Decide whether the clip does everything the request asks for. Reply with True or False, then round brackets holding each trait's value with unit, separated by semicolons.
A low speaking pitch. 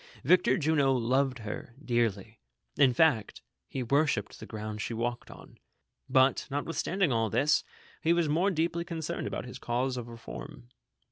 True (130 Hz)